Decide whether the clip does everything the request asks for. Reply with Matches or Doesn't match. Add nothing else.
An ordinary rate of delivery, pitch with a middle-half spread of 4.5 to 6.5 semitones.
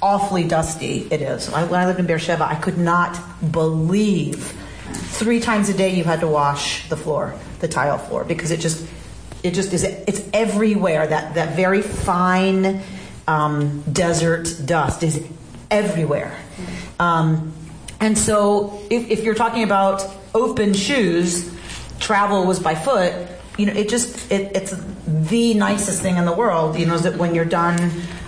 Doesn't match